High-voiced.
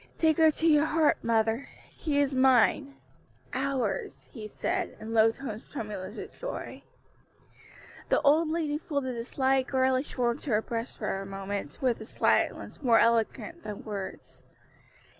Yes: very high, 255 Hz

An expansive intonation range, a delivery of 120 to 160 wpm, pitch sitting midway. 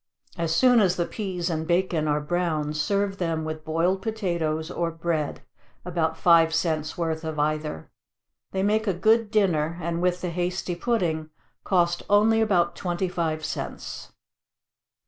No: average, 2.9 semitones; average, 150 wpm; medium, 170 Hz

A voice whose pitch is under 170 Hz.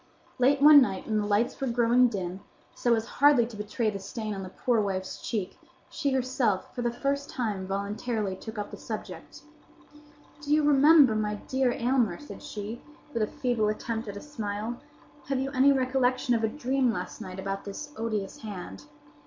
No: high, 230 Hz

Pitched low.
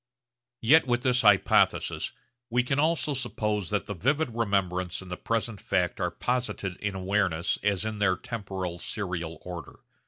Yes: low, 105 Hz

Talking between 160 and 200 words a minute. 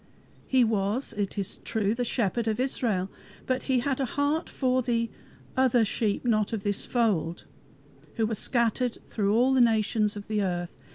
Yes: average, 170 wpm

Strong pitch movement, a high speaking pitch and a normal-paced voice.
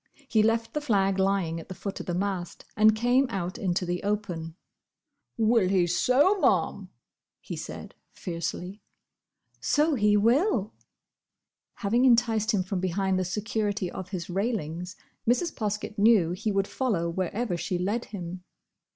No: average, 3.8 semitones; high, 200 Hz; average, 150 wpm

